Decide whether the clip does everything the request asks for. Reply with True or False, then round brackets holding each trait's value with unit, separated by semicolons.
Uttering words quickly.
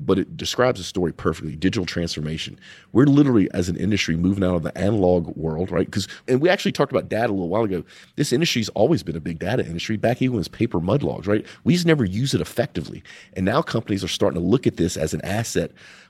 True (245 wpm)